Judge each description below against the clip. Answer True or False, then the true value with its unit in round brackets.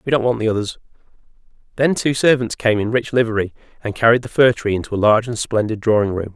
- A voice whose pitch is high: False (115 Hz)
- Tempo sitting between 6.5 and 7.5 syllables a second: True (6.6 syllables/s)